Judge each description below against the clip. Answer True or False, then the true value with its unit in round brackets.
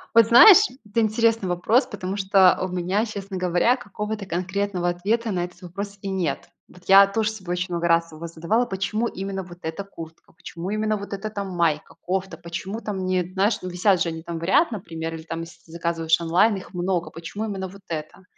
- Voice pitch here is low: False (190 Hz)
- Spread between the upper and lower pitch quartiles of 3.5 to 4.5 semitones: False (3.1 semitones)